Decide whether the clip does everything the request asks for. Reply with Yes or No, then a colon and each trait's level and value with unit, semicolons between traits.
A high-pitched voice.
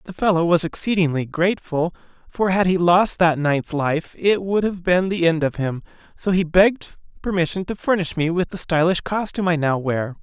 No: medium, 170 Hz